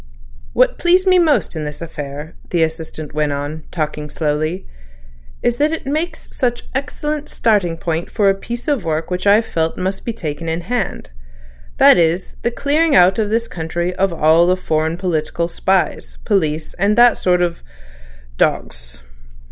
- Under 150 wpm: No, average, 165 wpm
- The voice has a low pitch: No, medium, 170 Hz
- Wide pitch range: Yes, wide, 6.3 semitones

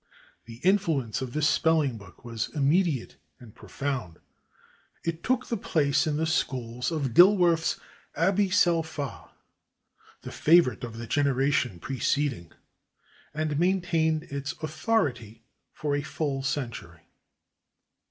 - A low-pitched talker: No, medium, 145 Hz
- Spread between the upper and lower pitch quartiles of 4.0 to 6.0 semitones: Yes, average, 4.9 semitones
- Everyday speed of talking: No, slow, 120 wpm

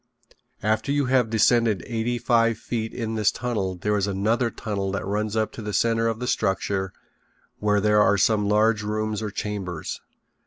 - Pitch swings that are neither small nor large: No, narrow, 2.0 semitones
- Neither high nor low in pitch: No, low, 110 Hz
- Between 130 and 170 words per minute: No, average, 180 wpm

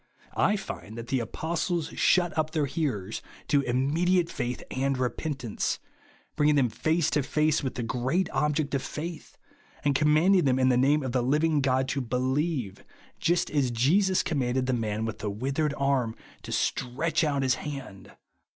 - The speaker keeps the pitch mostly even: No, average, 3.8 semitones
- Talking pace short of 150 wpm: No, average, 180 wpm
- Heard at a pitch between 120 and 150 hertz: Yes, medium, 140 Hz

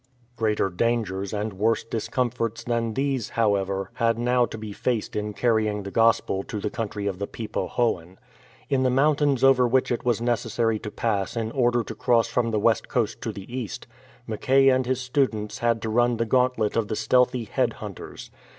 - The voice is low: Yes, low, 115 Hz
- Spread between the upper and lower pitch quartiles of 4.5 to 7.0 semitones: No, average, 2.7 semitones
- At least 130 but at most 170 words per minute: No, average, 195 wpm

